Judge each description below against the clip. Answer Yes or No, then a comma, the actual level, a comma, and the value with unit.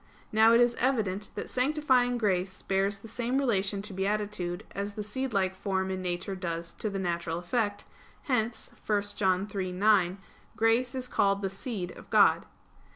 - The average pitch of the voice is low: No, high, 200 Hz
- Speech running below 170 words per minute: Yes, average, 160 wpm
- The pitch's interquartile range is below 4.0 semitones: Yes, average, 3.5 semitones